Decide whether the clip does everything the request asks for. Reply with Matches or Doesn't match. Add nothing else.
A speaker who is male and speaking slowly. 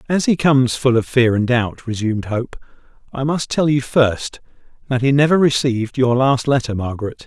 Doesn't match